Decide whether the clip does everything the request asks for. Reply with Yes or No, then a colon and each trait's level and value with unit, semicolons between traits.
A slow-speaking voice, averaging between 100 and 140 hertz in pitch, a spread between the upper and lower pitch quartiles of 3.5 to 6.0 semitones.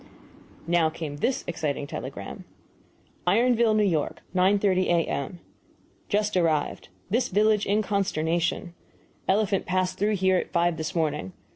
No: slow, 125 wpm; medium, 185 Hz; average, 4.0 semitones